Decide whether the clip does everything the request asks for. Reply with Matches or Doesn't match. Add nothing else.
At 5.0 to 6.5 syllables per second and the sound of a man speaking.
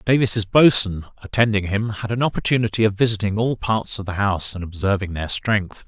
Matches